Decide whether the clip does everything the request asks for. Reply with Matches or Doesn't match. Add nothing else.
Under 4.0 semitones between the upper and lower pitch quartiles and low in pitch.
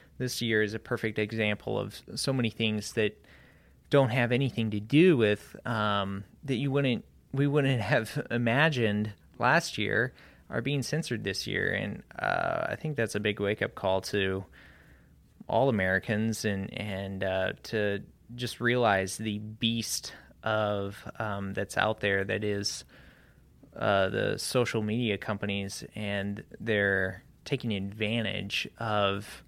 Matches